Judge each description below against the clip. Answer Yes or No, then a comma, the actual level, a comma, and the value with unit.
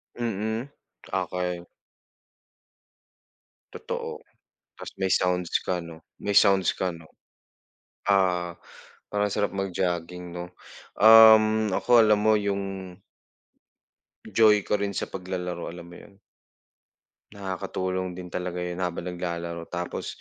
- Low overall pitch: Yes, very low, 95 Hz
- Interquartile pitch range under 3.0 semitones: Yes, narrow, 2.6 semitones